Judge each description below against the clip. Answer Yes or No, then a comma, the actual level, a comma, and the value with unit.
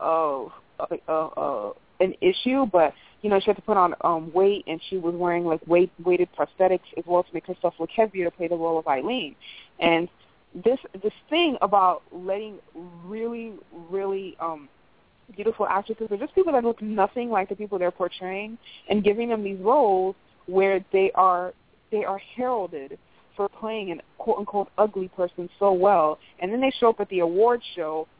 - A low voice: No, high, 190 Hz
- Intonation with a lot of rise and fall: No, average, 3.5 semitones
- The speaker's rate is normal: Yes, average, 185 wpm